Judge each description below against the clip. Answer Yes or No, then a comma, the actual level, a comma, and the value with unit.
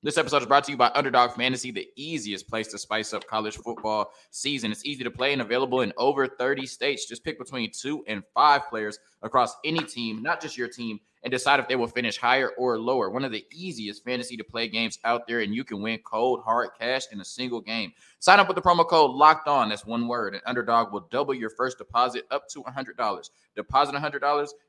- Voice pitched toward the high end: No, low, 125 Hz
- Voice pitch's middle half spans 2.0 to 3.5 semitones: No, average, 3.9 semitones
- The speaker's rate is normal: No, fast, 240 wpm